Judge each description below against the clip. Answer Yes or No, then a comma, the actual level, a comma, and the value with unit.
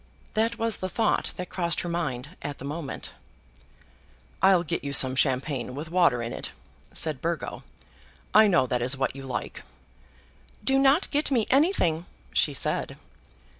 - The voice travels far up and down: Yes, wide, 7.9 semitones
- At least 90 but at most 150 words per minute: No, average, 160 wpm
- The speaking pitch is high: No, medium, 165 Hz